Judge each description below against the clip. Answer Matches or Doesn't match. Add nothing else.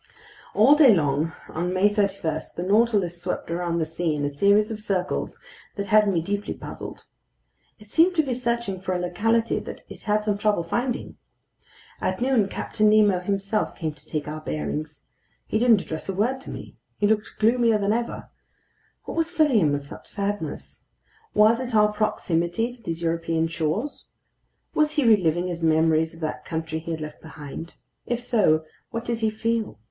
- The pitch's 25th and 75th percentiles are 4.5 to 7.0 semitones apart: Matches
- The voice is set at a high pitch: Matches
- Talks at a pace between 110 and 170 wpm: Doesn't match